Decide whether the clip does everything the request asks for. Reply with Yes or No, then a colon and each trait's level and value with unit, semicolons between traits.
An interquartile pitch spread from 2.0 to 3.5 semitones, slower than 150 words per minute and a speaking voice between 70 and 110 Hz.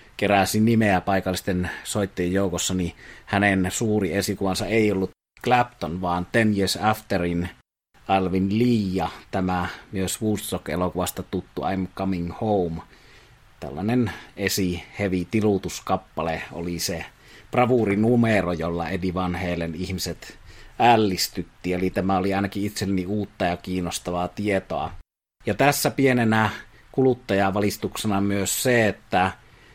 Yes: average, 2.9 semitones; average, 110 wpm; very low, 95 Hz